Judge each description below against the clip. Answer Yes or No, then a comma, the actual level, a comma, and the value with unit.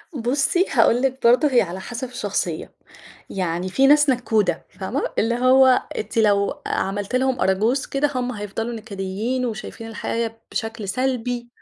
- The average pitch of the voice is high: Yes, high, 235 Hz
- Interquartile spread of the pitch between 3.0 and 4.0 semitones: Yes, average, 3.7 semitones